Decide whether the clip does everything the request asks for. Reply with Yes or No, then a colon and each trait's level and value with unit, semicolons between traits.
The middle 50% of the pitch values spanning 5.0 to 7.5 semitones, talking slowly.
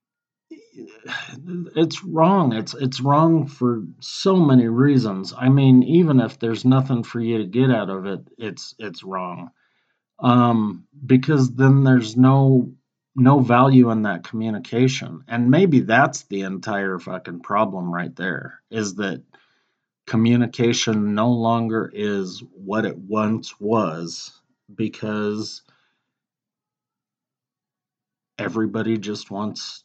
No: average, 3.8 semitones; slow, 115 wpm